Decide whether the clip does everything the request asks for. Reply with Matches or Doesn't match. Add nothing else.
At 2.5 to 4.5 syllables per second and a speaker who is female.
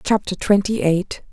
Matches